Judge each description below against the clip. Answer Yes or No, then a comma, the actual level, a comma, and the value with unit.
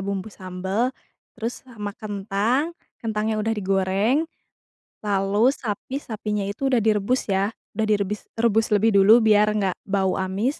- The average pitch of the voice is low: No, high, 210 Hz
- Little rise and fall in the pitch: Yes, narrow, 2.3 semitones